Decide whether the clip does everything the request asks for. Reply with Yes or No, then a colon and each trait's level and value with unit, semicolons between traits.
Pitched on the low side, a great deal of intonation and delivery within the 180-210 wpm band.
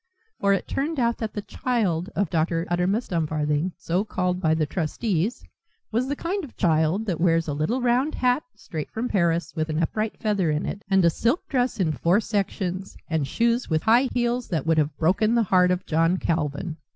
No: medium, 185 Hz; wide, 6.0 semitones; average, 200 wpm